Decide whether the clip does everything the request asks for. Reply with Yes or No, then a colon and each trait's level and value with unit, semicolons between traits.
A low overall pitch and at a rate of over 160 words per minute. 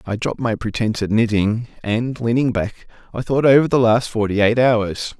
Yes: low, 115 Hz; average, 195 wpm